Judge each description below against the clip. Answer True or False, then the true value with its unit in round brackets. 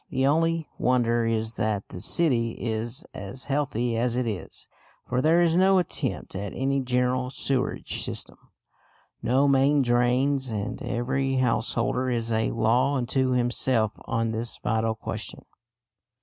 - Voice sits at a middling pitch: False (125 Hz)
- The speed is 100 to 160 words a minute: True (140 wpm)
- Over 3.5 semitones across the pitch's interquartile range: False (2.8 semitones)